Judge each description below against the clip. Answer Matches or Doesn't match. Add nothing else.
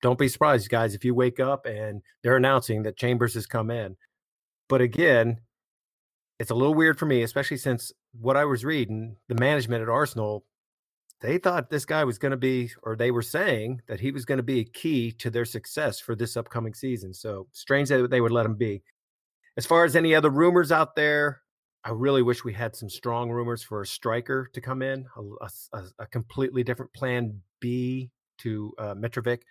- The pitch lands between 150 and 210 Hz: Doesn't match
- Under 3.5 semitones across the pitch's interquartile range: Matches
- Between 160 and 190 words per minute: Doesn't match